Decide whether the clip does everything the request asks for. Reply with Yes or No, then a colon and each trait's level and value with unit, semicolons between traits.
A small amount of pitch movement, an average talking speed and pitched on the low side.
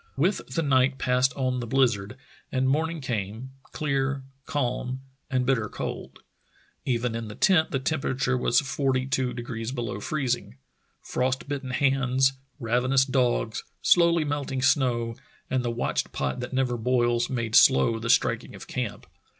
Yes: narrow, 2.1 semitones; average, 155 wpm; low, 130 Hz